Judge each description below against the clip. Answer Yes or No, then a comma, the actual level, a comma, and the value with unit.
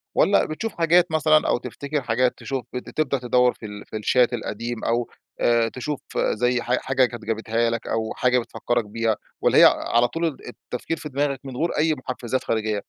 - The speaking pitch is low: Yes, low, 125 Hz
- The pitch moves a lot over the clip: No, average, 3.2 semitones